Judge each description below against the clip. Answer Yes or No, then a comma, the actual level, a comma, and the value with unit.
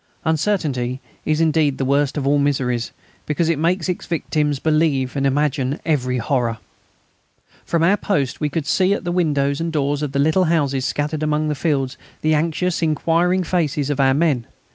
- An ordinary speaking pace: Yes, average, 185 wpm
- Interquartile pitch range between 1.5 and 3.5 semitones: Yes, average, 3.0 semitones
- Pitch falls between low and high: Yes, medium, 150 Hz